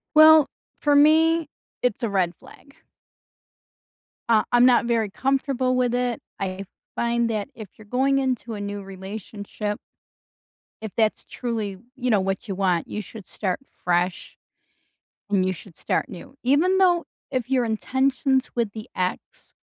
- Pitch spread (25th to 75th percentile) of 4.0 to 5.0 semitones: Yes, average, 4.6 semitones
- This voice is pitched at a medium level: No, high, 230 Hz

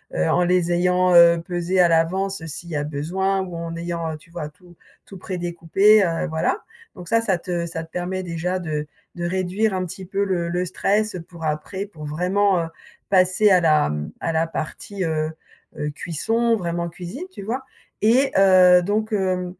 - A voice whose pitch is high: No, medium, 180 Hz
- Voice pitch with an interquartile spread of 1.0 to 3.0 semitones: Yes, narrow, 2.5 semitones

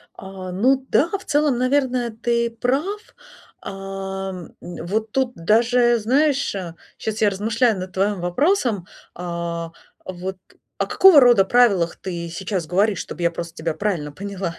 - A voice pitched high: Yes, high, 200 Hz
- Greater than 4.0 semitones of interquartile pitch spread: Yes, average, 5.3 semitones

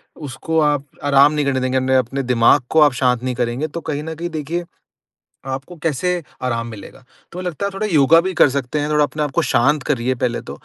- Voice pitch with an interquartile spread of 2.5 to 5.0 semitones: Yes, average, 3.5 semitones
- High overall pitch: No, medium, 140 Hz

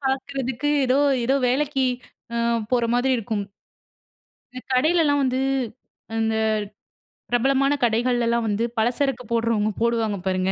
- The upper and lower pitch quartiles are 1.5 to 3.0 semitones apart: Yes, average, 2.7 semitones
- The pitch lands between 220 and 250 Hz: Yes, high, 245 Hz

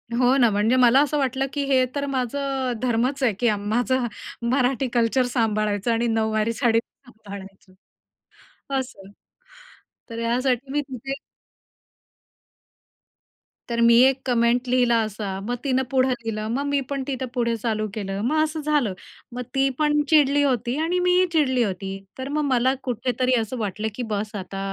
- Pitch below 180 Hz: No, high, 245 Hz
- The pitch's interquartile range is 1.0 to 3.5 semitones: Yes, average, 3.1 semitones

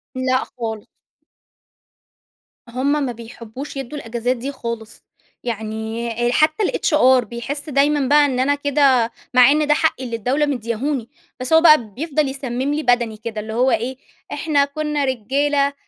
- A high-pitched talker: Yes, very high, 260 Hz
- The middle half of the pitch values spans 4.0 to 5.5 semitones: No, average, 3.6 semitones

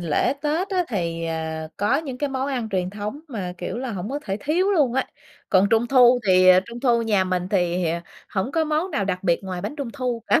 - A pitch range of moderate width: No, wide, 6.9 semitones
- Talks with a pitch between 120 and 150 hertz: No, high, 225 Hz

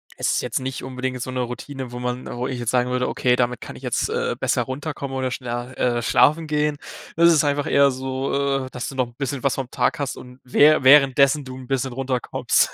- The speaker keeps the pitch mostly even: Yes, narrow, 1.9 semitones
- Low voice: Yes, low, 130 Hz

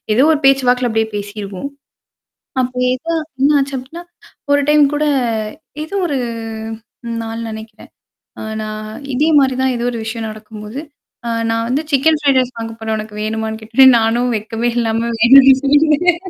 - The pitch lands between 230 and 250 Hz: Yes, high, 240 Hz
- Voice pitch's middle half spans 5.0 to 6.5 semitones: No, average, 3.8 semitones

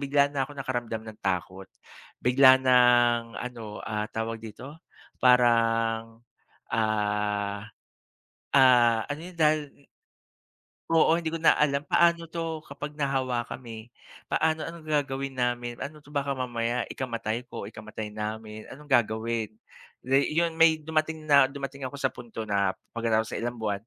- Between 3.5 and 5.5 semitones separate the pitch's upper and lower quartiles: Yes, average, 4.1 semitones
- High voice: No, low, 125 Hz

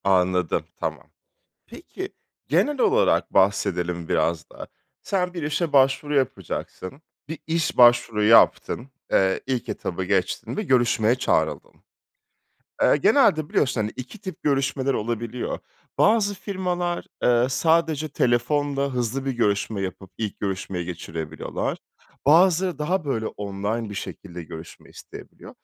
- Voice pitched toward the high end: No, low, 125 Hz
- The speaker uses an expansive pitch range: Yes, wide, 7.8 semitones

